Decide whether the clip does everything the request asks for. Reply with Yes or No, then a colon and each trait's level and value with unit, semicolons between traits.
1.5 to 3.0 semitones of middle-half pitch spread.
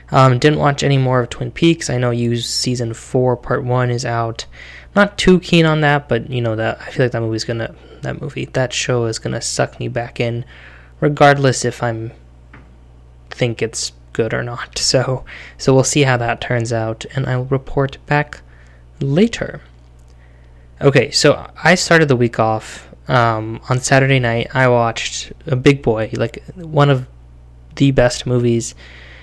No: average, 3.6 semitones